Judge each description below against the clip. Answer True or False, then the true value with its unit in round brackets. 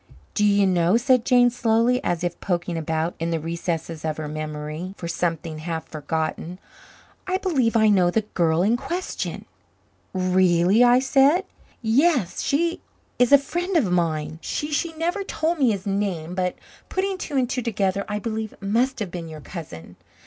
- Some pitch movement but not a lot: False (6.9 semitones)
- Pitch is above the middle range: True (195 Hz)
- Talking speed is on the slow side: False (180 wpm)